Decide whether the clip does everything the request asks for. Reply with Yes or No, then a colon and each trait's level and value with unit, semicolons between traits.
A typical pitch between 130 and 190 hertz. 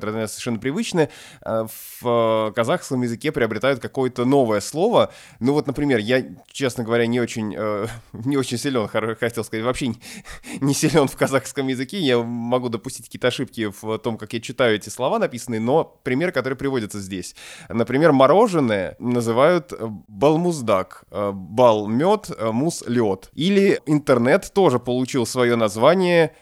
No: low, 120 Hz